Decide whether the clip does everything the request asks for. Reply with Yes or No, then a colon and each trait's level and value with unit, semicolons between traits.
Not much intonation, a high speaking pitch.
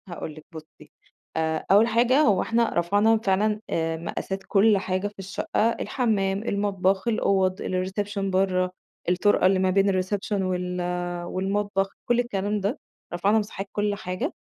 Yes: narrow, 2.1 semitones; high, 195 Hz